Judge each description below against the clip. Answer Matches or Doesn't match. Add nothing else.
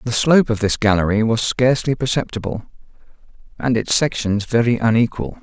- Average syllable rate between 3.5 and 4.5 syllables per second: Doesn't match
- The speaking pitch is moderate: Doesn't match